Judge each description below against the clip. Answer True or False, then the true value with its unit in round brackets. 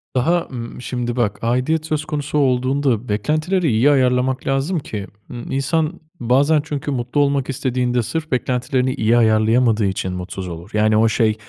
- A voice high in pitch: False (125 Hz)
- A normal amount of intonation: True (4.0 semitones)